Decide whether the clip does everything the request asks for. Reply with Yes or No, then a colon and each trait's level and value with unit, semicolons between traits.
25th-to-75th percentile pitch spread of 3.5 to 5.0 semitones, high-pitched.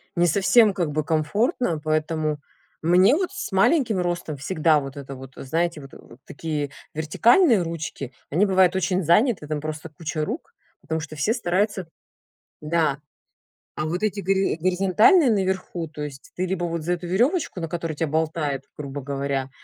No: average, 4.0 semitones; medium, 170 Hz